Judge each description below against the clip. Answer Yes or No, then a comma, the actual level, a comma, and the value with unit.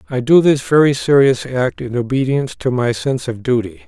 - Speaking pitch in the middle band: No, low, 130 Hz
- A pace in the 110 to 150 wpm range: No, average, 200 wpm